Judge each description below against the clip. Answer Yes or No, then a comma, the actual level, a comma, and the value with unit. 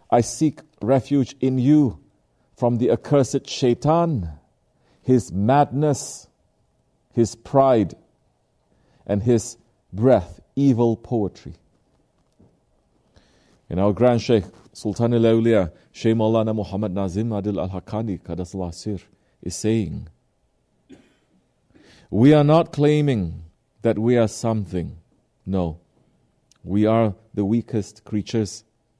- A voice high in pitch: No, low, 110 Hz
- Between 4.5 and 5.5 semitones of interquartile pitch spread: No, average, 4.0 semitones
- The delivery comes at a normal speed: No, slow, 95 wpm